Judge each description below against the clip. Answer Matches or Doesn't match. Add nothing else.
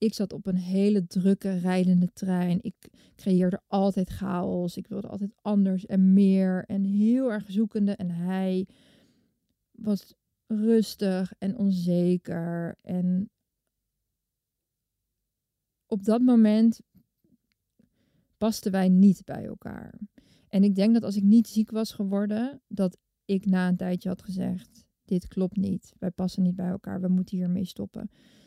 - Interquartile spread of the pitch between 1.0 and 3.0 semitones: Matches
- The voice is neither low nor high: Doesn't match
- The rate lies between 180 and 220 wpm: Doesn't match